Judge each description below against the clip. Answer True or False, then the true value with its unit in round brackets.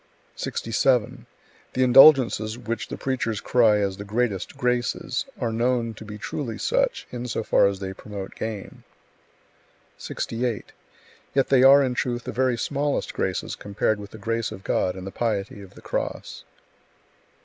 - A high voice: False (115 Hz)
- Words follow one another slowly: False (160 wpm)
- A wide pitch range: False (3.4 semitones)